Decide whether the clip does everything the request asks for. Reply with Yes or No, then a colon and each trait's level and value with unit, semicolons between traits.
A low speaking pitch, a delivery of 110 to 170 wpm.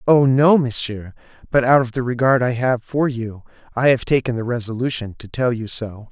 No: low, 125 Hz; fast, 205 wpm